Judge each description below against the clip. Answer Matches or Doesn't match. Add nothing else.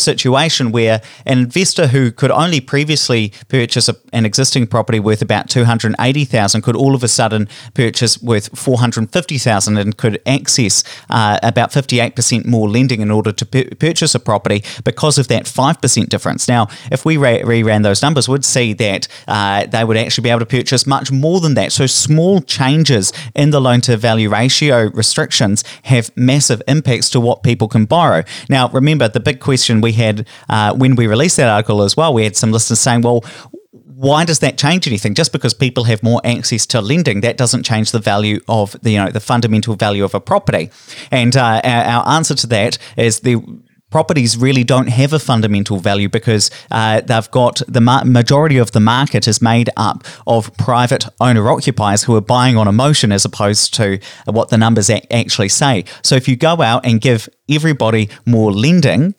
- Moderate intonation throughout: Matches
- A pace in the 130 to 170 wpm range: Doesn't match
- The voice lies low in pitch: Matches